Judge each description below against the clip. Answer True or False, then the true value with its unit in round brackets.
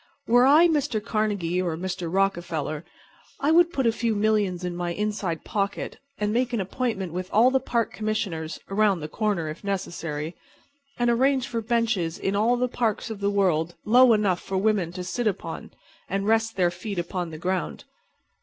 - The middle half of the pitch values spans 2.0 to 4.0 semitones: False (4.6 semitones)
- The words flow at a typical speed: True (180 wpm)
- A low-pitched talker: False (200 Hz)